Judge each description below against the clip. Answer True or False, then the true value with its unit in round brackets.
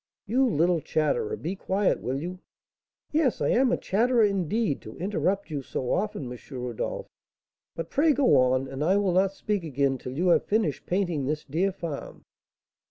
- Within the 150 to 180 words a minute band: True (175 wpm)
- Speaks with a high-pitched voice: False (180 Hz)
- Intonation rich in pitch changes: True (6.5 semitones)